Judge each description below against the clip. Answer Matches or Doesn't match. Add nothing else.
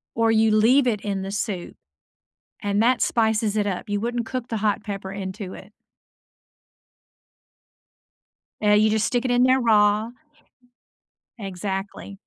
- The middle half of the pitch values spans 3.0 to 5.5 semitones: Doesn't match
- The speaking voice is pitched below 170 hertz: Doesn't match